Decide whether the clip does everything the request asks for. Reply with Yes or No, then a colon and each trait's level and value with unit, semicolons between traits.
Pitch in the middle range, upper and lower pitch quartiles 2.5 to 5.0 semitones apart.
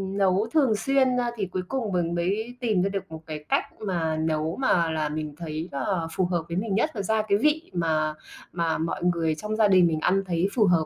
Yes: medium, 180 Hz; average, 4.7 semitones